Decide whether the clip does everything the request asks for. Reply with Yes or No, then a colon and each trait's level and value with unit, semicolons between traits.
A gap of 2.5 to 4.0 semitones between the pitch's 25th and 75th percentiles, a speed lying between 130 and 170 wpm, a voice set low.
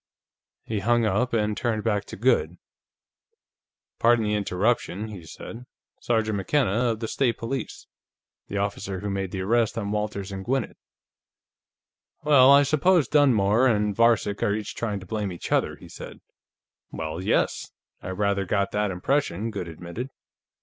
Yes: average, 3.2 semitones; average, 155 wpm; low, 105 Hz